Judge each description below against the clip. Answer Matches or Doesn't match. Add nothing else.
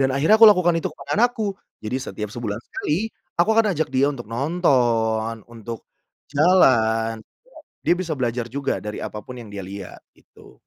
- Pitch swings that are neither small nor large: Doesn't match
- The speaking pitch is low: Matches